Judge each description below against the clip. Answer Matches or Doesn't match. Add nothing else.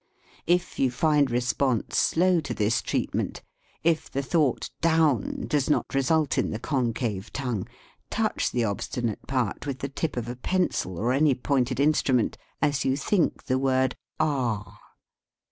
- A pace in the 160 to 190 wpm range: Doesn't match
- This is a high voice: Doesn't match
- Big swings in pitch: Doesn't match